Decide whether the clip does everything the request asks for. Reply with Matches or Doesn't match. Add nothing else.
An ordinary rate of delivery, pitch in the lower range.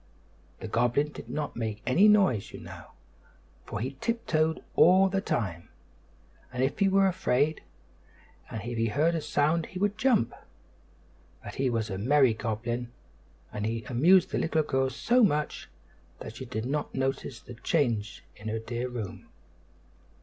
Matches